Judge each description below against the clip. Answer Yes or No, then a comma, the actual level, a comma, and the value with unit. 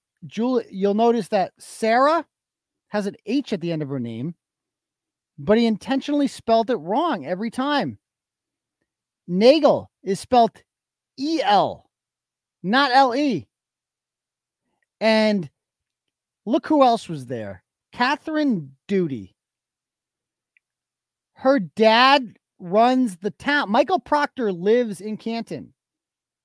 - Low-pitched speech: No, high, 220 Hz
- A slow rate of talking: Yes, slow, 105 wpm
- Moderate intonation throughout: No, wide, 7.4 semitones